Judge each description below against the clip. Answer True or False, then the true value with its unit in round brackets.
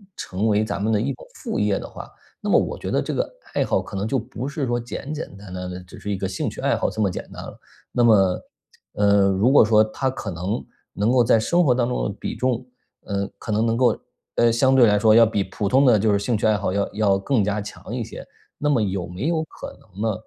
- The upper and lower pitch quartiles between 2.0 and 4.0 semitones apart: True (3.4 semitones)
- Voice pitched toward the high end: False (110 Hz)